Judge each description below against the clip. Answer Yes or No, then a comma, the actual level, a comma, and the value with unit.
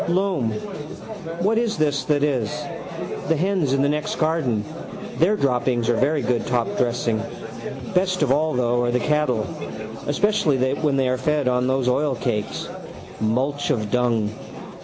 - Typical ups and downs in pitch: Yes, average, 4.0 semitones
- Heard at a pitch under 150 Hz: Yes, low, 135 Hz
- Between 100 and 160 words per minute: Yes, average, 150 wpm